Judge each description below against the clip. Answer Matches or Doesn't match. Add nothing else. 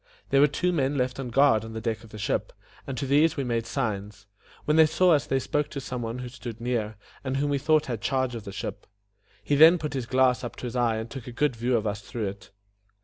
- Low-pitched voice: Matches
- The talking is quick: Matches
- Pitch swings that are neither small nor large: Matches